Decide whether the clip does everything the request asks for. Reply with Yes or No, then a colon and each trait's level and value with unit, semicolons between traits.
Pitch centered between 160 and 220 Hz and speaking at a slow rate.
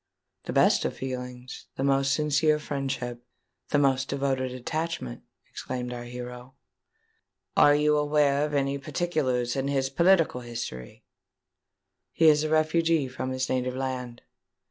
No: low, 135 Hz; slow, 120 wpm